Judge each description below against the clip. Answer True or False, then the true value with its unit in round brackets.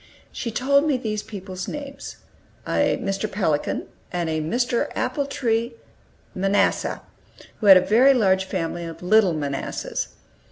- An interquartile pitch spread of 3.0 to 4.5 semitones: False (5.2 semitones)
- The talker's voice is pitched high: True (205 Hz)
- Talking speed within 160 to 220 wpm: False (135 wpm)